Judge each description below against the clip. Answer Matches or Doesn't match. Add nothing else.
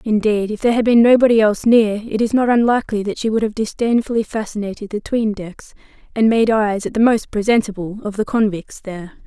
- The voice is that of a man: Doesn't match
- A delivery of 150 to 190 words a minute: Doesn't match